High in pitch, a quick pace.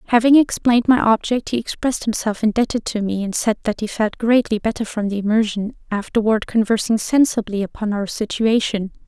No: high, 220 Hz; average, 170 wpm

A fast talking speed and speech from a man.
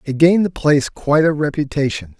No: average, 190 wpm; male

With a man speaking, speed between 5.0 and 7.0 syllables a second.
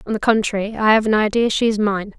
No: female; 6.4 syllables/s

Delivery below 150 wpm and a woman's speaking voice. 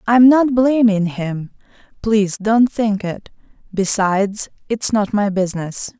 Yes: average, 140 wpm; female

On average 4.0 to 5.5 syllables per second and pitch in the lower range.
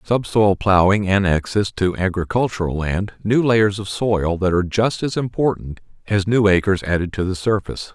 Yes: 4.9 syllables/s; low, 100 Hz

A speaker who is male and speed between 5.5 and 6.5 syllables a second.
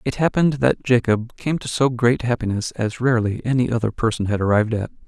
Yes: male; 6.0 syllables/s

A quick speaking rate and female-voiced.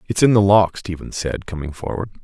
No: fast, 215 wpm; male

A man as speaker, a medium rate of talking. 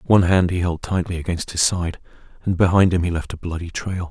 No: male; fast, 235 wpm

